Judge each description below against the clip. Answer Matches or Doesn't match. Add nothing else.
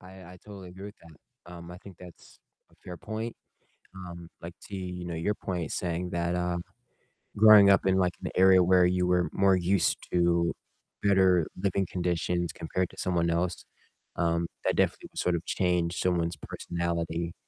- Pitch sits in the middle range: Doesn't match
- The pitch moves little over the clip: Matches